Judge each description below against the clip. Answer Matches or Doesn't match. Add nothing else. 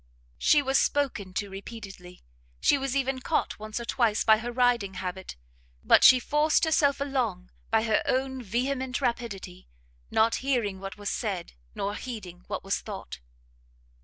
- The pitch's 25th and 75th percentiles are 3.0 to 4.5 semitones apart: Doesn't match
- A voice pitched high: Matches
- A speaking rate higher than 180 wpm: Doesn't match